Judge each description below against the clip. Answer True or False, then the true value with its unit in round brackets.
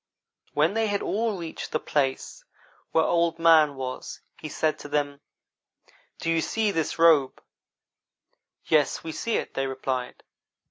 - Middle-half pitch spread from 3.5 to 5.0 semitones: False (2.8 semitones)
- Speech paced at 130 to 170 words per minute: True (145 wpm)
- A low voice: False (160 Hz)